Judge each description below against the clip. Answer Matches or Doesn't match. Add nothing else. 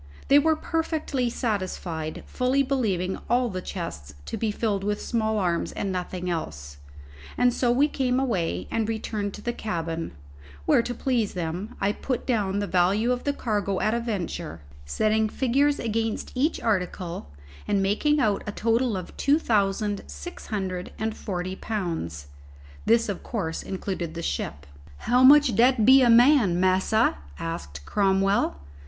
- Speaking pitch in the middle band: Doesn't match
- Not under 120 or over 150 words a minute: Doesn't match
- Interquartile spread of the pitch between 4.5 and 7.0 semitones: Matches